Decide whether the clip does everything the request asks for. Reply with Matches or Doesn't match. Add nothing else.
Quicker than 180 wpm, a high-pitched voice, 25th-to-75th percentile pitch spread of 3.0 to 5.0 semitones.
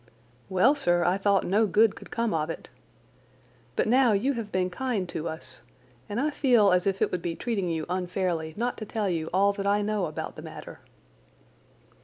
Matches